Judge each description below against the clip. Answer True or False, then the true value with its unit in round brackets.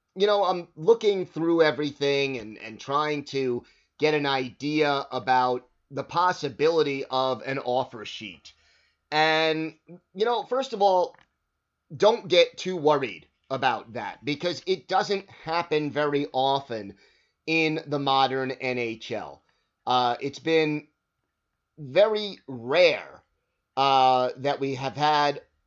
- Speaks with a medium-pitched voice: True (145 Hz)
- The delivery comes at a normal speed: False (120 wpm)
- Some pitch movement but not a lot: True (4.5 semitones)